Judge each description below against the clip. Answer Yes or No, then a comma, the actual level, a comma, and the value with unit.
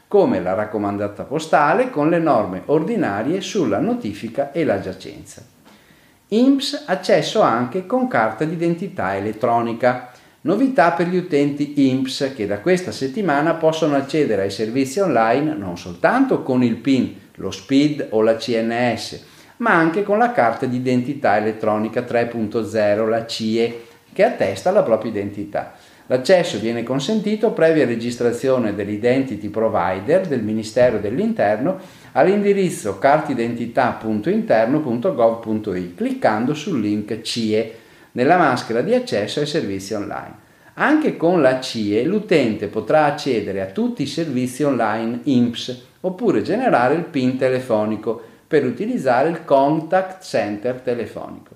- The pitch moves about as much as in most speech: No, wide, 6.0 semitones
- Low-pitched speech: Yes, low, 125 Hz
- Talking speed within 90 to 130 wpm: Yes, average, 125 wpm